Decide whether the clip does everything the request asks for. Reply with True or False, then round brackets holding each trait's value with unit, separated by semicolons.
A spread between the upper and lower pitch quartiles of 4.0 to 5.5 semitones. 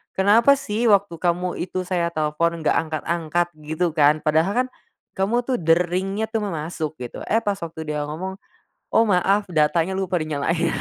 False (3.5 semitones)